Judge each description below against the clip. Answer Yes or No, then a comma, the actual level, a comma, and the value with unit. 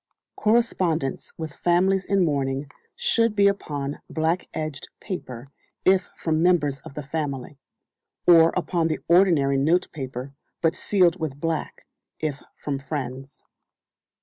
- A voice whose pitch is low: No, medium, 160 Hz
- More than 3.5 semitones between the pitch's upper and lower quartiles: Yes, average, 4.5 semitones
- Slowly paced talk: Yes, slow, 120 wpm